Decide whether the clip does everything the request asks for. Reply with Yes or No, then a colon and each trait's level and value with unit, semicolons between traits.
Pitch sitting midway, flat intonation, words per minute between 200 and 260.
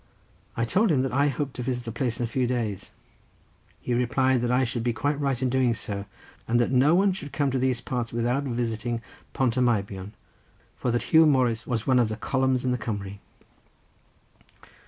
No: low, 125 Hz; narrow, 2.3 semitones; fast, 205 wpm